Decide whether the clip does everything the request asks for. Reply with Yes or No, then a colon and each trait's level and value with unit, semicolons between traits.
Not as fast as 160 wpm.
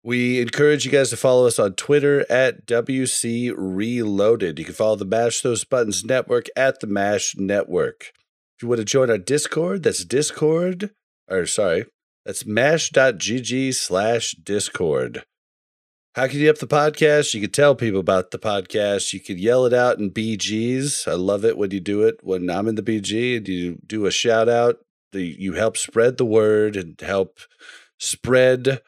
No: average, 175 wpm